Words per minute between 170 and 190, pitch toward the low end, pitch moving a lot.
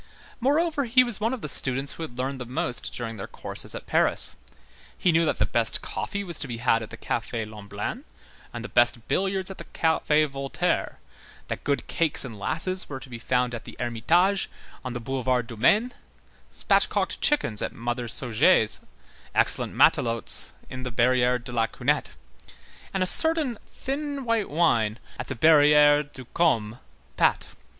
Yes: average, 175 wpm; low, 130 Hz; wide, 7.6 semitones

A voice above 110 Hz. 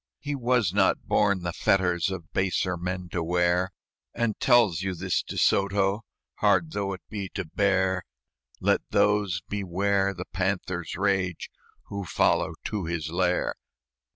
No: very low, 95 Hz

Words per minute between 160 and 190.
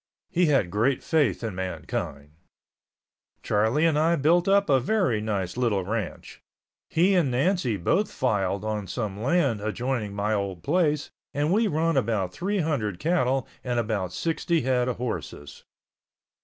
No: average, 150 wpm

